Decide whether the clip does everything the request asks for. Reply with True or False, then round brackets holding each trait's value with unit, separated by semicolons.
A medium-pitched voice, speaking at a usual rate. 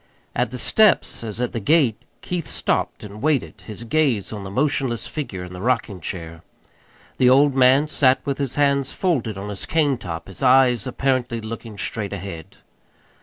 False (120 Hz; 170 wpm)